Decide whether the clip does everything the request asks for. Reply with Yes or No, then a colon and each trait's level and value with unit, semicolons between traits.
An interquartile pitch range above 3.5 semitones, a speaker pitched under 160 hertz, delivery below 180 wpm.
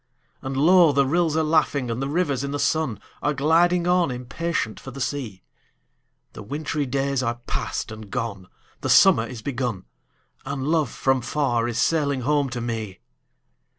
Yes: average, 4.3 semitones; low, 135 Hz; average, 170 wpm